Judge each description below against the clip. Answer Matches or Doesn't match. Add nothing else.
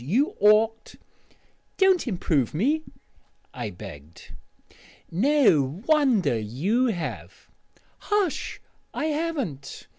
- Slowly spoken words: Matches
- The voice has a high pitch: Matches